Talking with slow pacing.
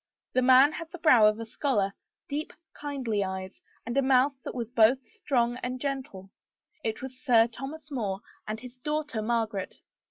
No: average, 170 wpm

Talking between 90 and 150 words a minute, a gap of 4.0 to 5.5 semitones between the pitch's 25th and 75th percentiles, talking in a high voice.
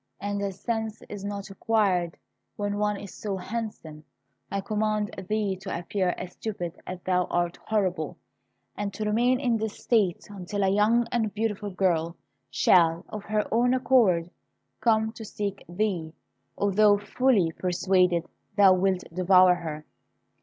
No: average, 145 wpm; average, 3.0 semitones; high, 200 Hz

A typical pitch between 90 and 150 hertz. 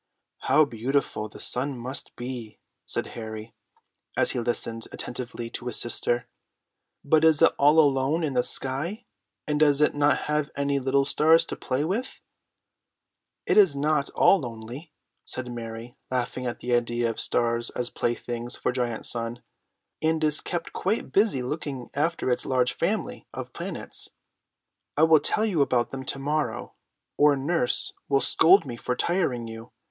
Yes: low, 135 Hz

